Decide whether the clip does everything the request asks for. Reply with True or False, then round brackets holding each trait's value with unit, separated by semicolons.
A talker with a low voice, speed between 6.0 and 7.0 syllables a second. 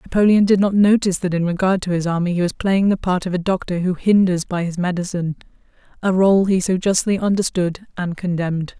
False (185 Hz; 6.1 syllables/s)